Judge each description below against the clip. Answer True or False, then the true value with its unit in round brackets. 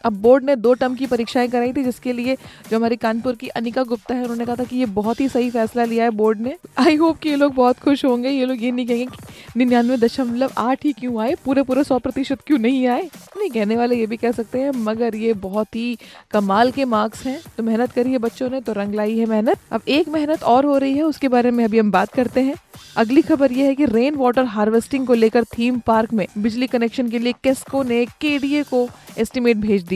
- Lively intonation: False (2.5 semitones)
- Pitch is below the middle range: False (245 Hz)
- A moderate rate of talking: False (245 wpm)